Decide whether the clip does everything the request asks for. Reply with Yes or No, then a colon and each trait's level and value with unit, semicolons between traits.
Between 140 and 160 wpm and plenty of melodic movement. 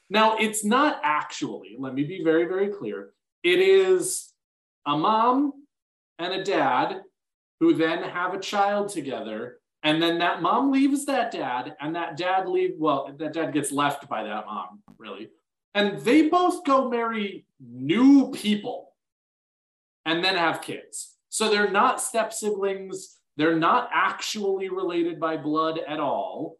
Yes: average, 150 wpm; wide, 8.7 semitones